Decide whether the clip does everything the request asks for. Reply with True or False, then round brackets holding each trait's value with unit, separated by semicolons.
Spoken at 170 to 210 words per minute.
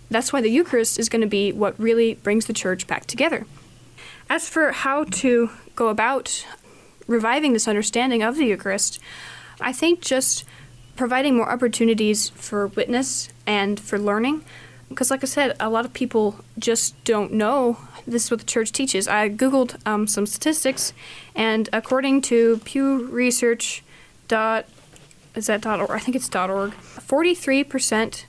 False (160 wpm)